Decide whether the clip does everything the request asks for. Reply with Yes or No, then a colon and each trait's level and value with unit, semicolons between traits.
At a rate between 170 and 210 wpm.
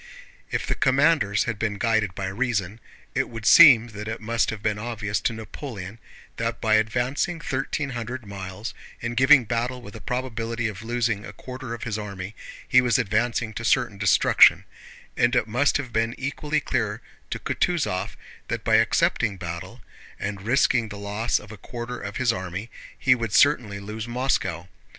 Yes: average, 175 wpm